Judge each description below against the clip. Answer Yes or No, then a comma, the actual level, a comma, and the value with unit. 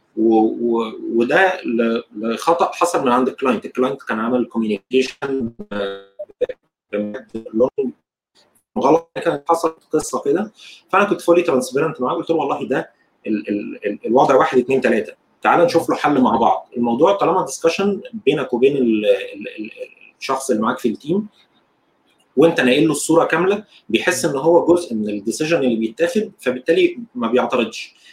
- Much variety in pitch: Yes, wide, 7.6 semitones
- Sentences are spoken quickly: Yes, fast, 145 wpm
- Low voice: No, medium, 155 Hz